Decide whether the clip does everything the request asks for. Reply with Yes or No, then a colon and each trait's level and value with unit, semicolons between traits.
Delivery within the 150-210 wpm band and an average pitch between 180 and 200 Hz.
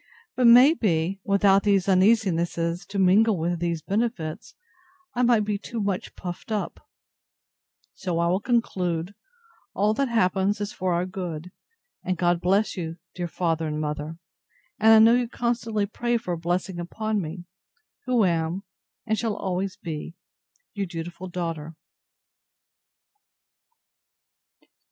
No: average, 140 wpm; high, 190 Hz